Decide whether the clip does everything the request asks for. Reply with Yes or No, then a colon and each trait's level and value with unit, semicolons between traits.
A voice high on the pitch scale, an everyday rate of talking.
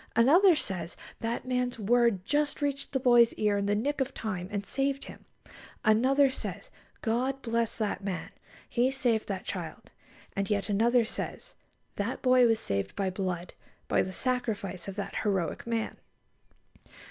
Yes: high, 230 Hz; average, 160 wpm